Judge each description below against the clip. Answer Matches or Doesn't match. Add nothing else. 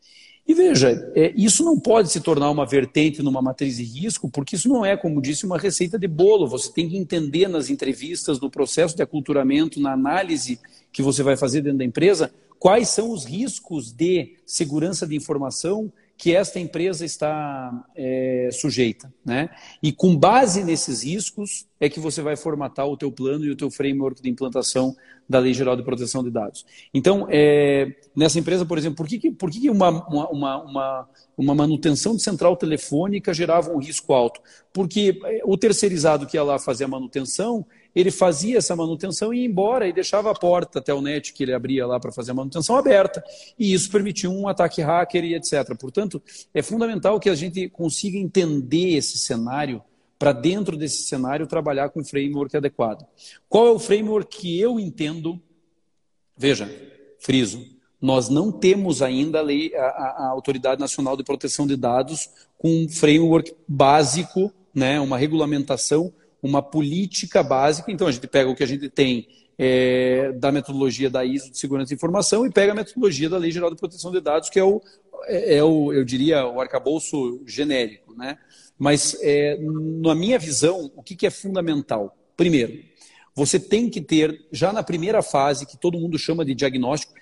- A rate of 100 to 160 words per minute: Doesn't match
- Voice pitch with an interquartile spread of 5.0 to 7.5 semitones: Matches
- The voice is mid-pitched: Matches